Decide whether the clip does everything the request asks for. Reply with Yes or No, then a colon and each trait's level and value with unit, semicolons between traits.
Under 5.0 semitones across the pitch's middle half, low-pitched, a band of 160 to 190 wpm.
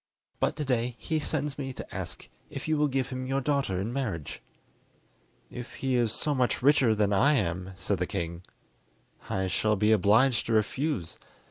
No: average, 5.3 semitones; low, 120 Hz; average, 185 wpm